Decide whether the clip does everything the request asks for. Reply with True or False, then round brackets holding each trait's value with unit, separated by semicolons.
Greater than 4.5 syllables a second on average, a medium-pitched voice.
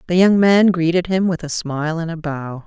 True (5.2 syllables/s; 170 Hz)